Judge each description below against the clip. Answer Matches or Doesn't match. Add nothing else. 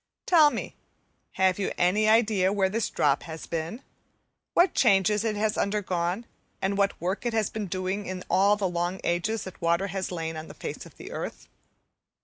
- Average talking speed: Matches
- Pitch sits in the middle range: Doesn't match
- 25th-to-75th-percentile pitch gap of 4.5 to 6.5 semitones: Doesn't match